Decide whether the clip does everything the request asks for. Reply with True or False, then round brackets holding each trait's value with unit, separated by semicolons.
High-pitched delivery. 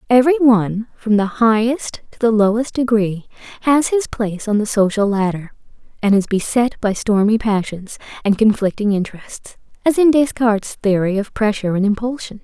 True (220 Hz)